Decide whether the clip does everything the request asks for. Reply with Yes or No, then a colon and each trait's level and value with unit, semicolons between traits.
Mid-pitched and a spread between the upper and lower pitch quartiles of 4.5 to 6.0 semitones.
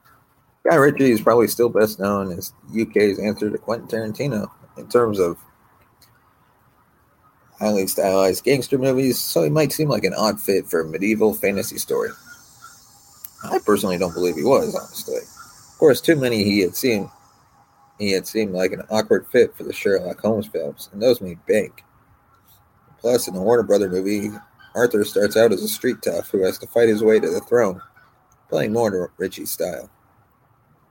No: low, 110 Hz; average, 5.1 semitones